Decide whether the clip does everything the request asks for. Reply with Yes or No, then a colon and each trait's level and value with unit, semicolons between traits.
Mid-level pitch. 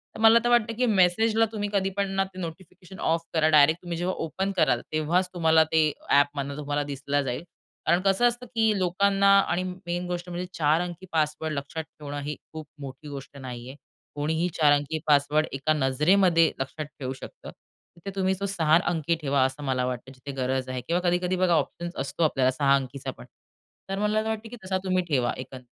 Yes: medium, 160 Hz